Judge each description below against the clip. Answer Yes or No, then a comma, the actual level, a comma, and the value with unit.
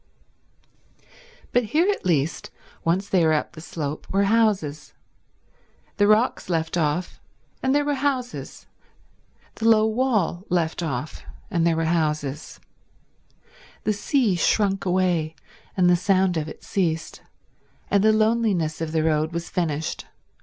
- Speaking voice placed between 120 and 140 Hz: No, medium, 180 Hz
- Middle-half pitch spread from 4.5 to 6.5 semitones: Yes, average, 5.1 semitones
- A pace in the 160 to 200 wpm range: No, average, 140 wpm